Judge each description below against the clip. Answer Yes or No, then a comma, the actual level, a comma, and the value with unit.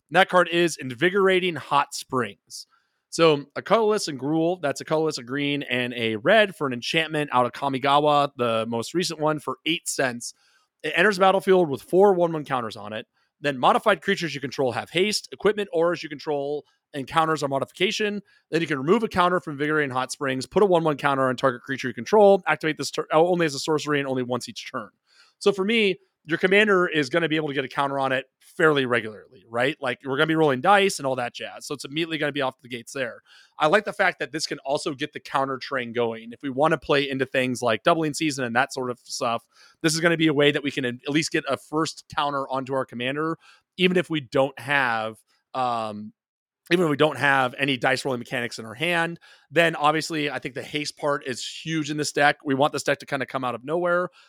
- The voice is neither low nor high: Yes, medium, 150 Hz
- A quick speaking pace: Yes, fast, 240 wpm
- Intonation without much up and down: No, average, 3.9 semitones